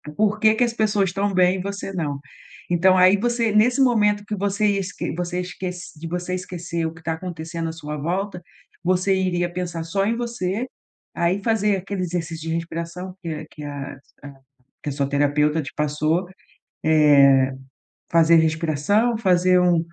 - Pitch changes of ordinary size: Yes, average, 3.5 semitones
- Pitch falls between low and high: Yes, medium, 180 Hz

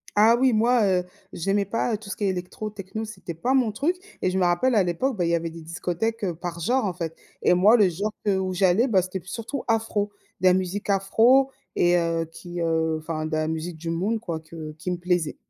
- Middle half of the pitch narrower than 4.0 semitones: No, average, 4.3 semitones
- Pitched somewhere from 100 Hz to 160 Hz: No, medium, 185 Hz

